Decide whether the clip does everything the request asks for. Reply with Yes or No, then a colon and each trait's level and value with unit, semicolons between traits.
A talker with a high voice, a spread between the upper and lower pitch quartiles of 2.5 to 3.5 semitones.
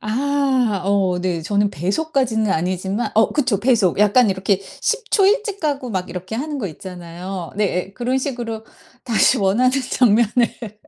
No: high, 215 Hz; average, 5.1 semitones